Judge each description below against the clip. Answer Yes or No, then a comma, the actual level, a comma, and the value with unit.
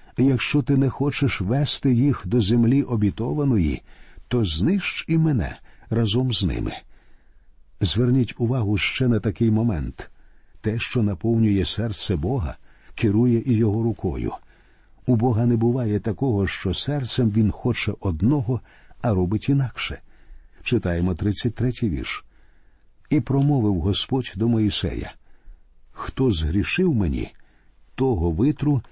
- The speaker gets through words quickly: No, average, 120 wpm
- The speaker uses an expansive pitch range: No, average, 4.1 semitones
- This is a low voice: Yes, low, 115 Hz